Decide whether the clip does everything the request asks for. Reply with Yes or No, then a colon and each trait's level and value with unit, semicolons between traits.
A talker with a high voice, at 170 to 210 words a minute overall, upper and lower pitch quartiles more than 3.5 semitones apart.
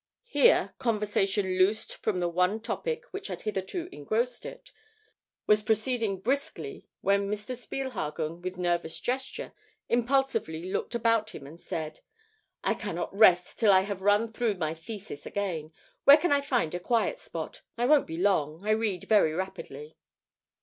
No: high, 205 Hz; average, 155 wpm; average, 5.1 semitones